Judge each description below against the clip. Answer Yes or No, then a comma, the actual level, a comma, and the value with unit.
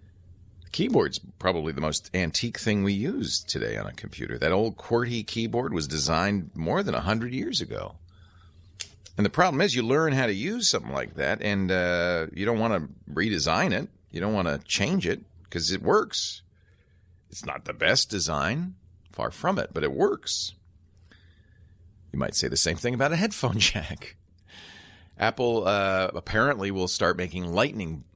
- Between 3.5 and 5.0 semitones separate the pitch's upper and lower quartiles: No, average, 2.7 semitones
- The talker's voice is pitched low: Yes, very low, 95 Hz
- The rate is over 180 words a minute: No, average, 175 wpm